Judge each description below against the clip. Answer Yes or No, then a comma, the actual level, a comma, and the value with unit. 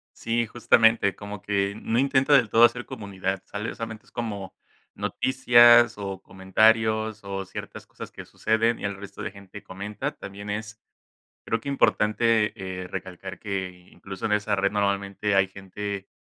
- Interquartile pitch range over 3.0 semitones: No, narrow, 2.5 semitones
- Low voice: Yes, low, 105 Hz